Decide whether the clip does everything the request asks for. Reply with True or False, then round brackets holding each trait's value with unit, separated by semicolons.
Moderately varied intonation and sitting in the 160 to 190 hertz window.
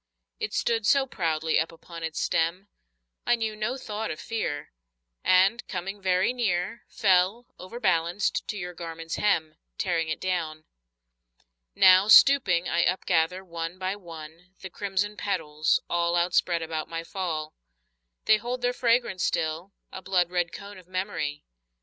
True (3.8 semitones; 185 Hz)